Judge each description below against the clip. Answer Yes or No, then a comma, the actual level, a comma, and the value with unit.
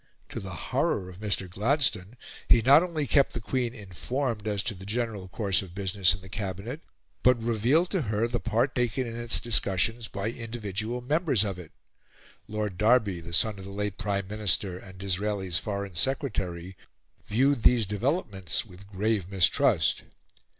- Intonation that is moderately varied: Yes, average, 3.9 semitones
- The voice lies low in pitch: Yes, low, 105 Hz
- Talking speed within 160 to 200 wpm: Yes, average, 165 wpm